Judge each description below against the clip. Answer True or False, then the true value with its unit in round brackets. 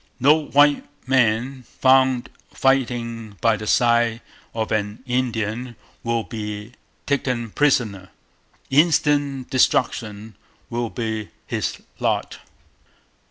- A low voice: True (120 Hz)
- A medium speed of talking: False (95 wpm)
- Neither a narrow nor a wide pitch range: True (3.1 semitones)